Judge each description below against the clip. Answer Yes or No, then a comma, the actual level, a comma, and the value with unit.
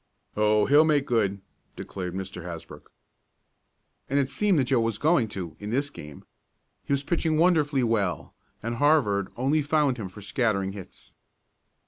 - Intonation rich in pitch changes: Yes, wide, 6.4 semitones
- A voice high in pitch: No, low, 120 Hz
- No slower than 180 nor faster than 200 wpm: No, average, 155 wpm